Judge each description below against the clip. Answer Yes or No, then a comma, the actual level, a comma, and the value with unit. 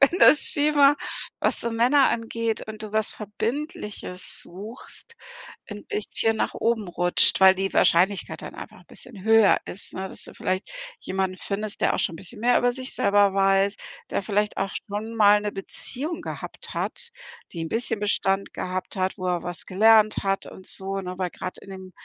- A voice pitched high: Yes, high, 205 Hz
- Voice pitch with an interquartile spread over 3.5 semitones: No, average, 3.0 semitones